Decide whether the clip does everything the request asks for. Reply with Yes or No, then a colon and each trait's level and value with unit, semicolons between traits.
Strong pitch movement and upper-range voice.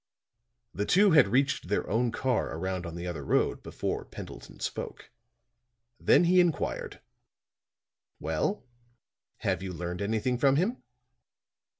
No: wide, 8.3 semitones; low, 110 Hz